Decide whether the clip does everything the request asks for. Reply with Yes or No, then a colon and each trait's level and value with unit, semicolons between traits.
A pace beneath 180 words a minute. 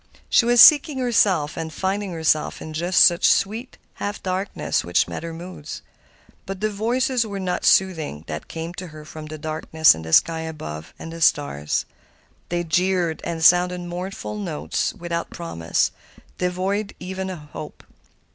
Yes: average, 160 wpm